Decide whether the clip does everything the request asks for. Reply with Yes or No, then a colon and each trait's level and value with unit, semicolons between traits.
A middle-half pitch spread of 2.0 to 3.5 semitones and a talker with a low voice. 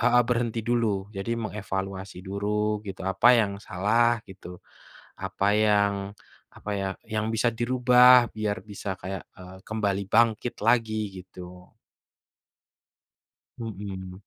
Yes: average, 3.2 semitones; low, 105 Hz